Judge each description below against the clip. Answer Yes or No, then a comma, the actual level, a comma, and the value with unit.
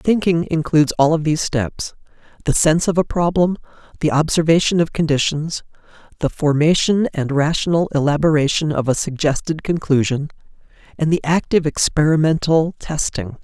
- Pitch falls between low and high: Yes, medium, 155 Hz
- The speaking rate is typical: No, slow, 125 wpm